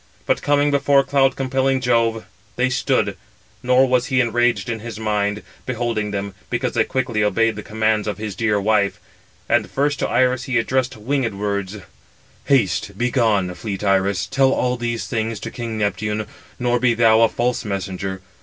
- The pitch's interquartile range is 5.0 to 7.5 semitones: No, average, 3.4 semitones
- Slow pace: No, average, 170 wpm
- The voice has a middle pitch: No, low, 115 Hz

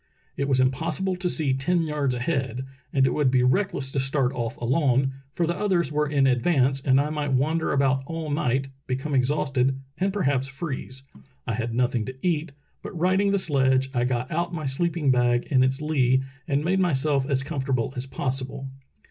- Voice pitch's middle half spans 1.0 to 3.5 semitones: Yes, average, 3.1 semitones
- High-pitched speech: No, low, 135 Hz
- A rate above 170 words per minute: Yes, average, 195 wpm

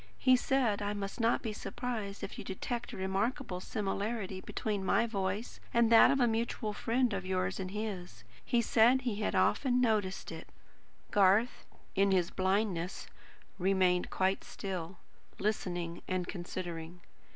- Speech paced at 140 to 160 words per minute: Yes, average, 150 wpm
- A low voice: No, high, 200 Hz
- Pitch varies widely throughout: No, average, 3.6 semitones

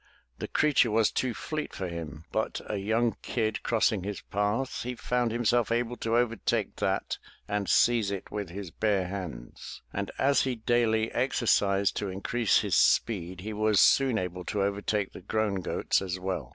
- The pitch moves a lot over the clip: No, average, 3.4 semitones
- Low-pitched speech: Yes, low, 105 Hz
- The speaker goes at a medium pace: Yes, average, 175 wpm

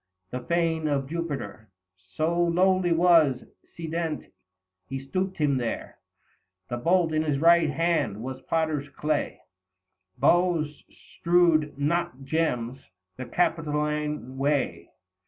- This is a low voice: No, medium, 155 Hz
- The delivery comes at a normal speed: No, slow, 110 wpm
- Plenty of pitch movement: No, average, 3.8 semitones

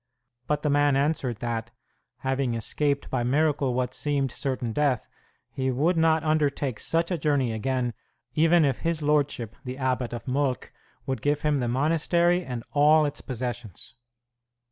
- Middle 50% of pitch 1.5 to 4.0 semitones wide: Yes, average, 3.1 semitones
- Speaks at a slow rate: No, average, 155 wpm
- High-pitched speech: No, medium, 140 Hz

